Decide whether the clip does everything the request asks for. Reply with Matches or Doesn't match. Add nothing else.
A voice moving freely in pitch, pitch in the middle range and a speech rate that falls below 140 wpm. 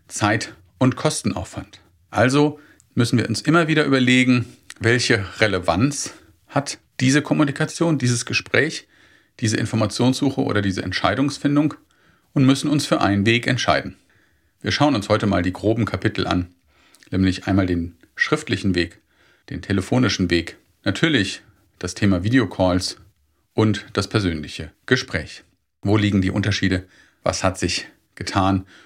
Doesn't match